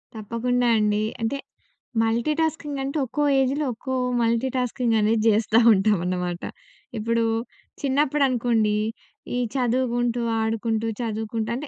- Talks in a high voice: Yes, high, 230 Hz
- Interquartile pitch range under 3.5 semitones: Yes, average, 2.9 semitones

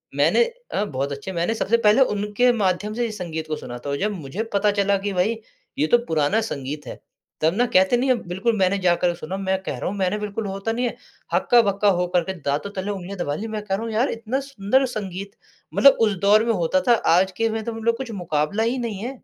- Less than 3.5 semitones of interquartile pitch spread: No, average, 4.0 semitones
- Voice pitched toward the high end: Yes, high, 200 Hz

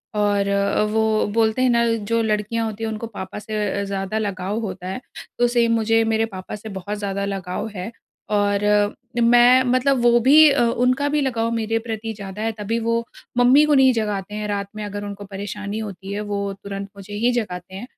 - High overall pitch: Yes, high, 215 Hz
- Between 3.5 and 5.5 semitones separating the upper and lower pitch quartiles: No, narrow, 2.5 semitones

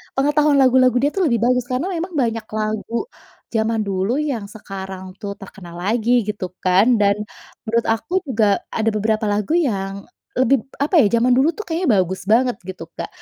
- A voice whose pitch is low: No, high, 225 Hz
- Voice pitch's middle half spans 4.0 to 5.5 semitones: Yes, average, 4.3 semitones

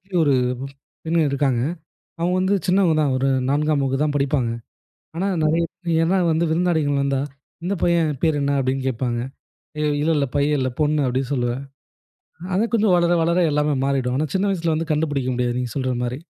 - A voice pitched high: No, medium, 150 Hz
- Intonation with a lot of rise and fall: No, average, 3.9 semitones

